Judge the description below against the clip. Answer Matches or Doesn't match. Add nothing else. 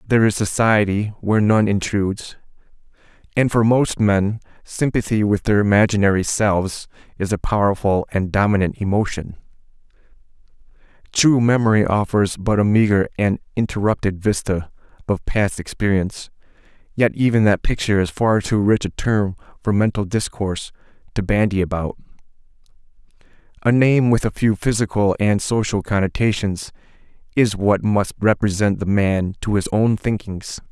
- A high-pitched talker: Doesn't match